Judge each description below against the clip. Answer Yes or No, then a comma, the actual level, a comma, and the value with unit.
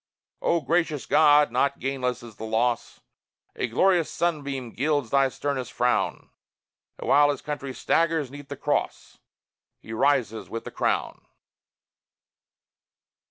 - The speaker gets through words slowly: Yes, slow, 125 wpm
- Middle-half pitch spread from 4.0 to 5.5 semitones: No, average, 3.1 semitones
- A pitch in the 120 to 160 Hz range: Yes, medium, 140 Hz